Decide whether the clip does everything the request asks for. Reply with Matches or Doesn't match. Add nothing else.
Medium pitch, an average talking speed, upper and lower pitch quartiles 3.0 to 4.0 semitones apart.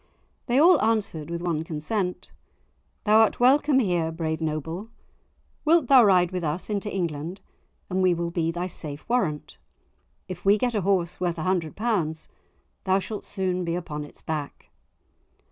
Doesn't match